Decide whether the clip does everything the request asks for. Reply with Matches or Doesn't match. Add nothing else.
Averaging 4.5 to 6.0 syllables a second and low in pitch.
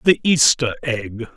Doesn't match